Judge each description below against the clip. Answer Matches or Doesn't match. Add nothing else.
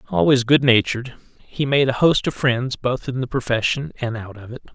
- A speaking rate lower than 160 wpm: Doesn't match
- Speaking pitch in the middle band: Doesn't match